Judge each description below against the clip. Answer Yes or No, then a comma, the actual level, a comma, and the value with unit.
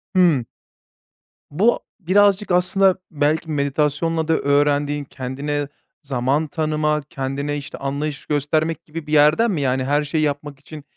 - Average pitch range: No, narrow, 2.2 semitones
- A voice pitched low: No, medium, 150 Hz